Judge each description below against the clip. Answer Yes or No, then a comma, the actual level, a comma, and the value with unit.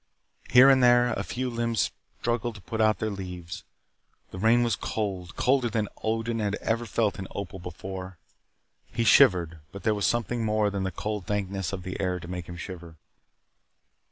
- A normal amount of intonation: Yes, average, 3.8 semitones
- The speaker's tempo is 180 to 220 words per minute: Yes, average, 185 wpm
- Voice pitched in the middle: No, low, 105 Hz